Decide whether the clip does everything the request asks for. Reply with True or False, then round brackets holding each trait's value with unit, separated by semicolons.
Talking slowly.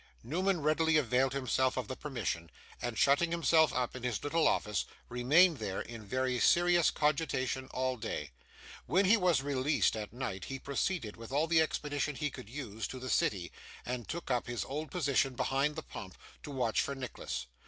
False (185 wpm)